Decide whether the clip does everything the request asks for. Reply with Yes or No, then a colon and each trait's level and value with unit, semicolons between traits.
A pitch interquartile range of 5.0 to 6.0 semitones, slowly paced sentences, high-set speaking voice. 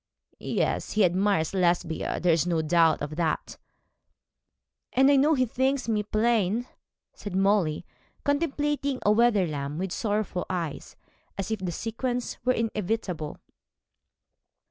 Yes: wide, 5.6 semitones; slow, 120 wpm; high, 205 Hz